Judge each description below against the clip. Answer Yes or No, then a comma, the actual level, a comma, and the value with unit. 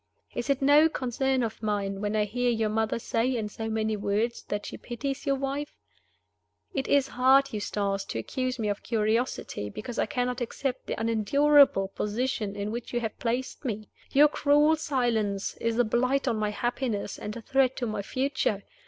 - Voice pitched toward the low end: No, high, 235 Hz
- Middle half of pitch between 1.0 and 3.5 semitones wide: No, average, 3.9 semitones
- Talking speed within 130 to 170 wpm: No, average, 185 wpm